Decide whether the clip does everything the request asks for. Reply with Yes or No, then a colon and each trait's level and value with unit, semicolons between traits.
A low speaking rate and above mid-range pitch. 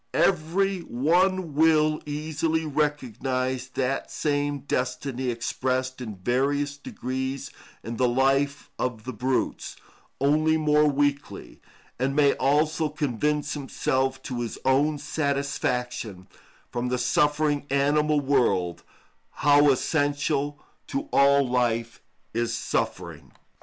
No: slow, 105 wpm; medium, 140 Hz